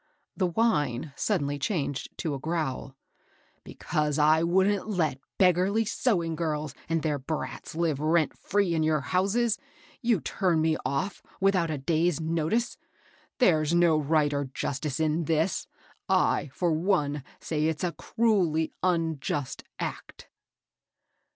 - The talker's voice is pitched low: No, medium, 160 Hz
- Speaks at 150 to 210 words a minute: No, average, 140 wpm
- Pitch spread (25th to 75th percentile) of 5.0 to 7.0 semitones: No, average, 3.4 semitones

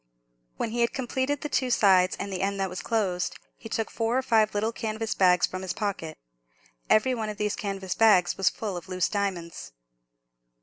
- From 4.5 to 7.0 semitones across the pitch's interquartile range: No, average, 3.4 semitones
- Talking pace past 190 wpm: Yes, average, 200 wpm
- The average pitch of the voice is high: Yes, high, 205 Hz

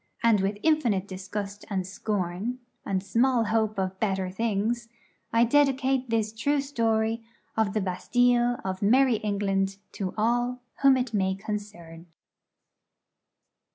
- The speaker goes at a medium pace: No, slow, 125 wpm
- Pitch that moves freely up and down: No, average, 3.8 semitones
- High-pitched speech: Yes, high, 215 Hz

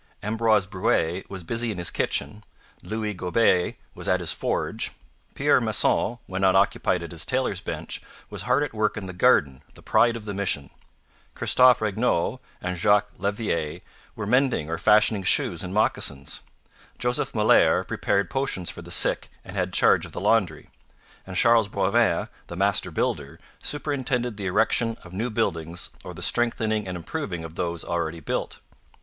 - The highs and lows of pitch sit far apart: No, average, 4.3 semitones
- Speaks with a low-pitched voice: Yes, low, 100 Hz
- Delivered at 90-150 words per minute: No, average, 165 wpm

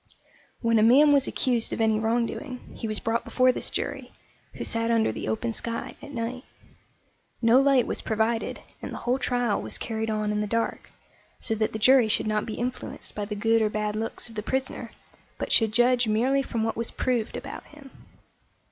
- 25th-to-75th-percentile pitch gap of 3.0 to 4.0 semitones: No, narrow, 2.4 semitones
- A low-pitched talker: No, high, 230 Hz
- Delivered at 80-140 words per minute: No, average, 200 wpm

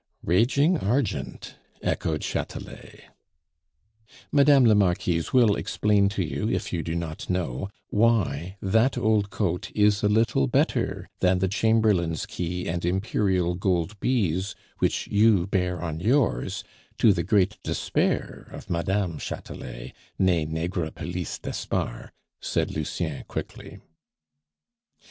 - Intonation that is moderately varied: Yes, average, 3.9 semitones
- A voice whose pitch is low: Yes, very low, 95 Hz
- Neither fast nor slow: No, slow, 120 wpm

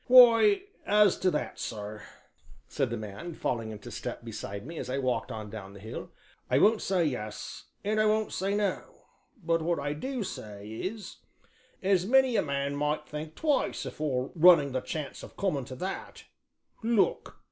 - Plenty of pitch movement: Yes, wide, 8.6 semitones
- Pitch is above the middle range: No, medium, 155 Hz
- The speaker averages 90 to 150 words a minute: No, average, 175 wpm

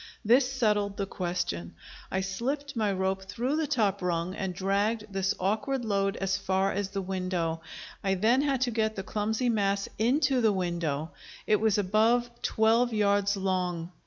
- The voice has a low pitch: No, high, 200 Hz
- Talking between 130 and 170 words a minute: Yes, average, 165 wpm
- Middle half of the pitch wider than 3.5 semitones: No, average, 3.1 semitones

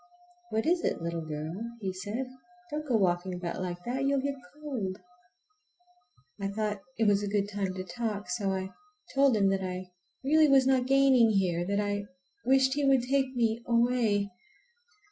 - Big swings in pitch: Yes, wide, 5.7 semitones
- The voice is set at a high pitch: Yes, high, 215 Hz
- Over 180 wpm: No, average, 175 wpm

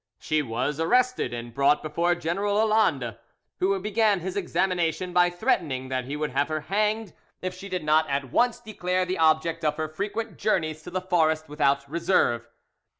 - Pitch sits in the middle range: Yes, medium, 170 Hz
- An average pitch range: Yes, average, 4.4 semitones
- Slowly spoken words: No, average, 175 wpm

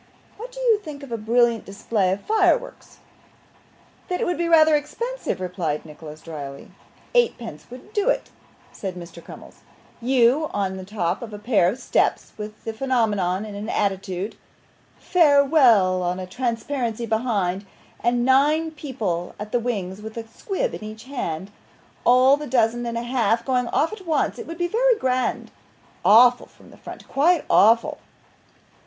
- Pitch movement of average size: No, wide, 6.4 semitones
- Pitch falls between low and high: No, high, 235 Hz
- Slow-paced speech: No, average, 165 wpm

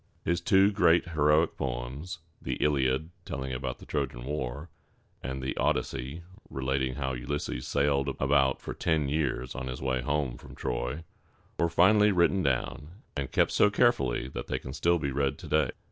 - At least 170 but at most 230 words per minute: Yes, average, 175 wpm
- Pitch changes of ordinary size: Yes, average, 3.8 semitones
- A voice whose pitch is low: Yes, very low, 70 Hz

